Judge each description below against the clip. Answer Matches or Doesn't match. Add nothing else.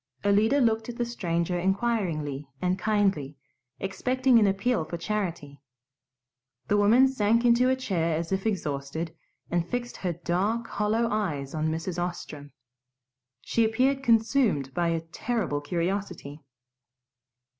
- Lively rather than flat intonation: Matches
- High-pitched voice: Matches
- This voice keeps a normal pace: Doesn't match